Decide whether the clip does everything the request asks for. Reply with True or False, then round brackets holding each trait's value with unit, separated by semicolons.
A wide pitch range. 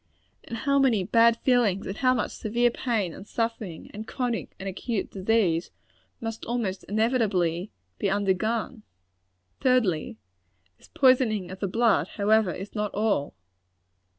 False (3.6 semitones)